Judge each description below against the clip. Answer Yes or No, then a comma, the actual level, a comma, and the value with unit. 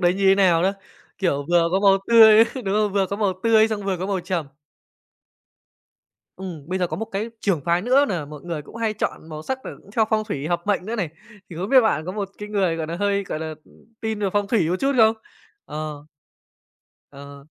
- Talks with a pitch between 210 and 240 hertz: No, high, 195 Hz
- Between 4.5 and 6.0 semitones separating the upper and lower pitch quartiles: No, average, 4.1 semitones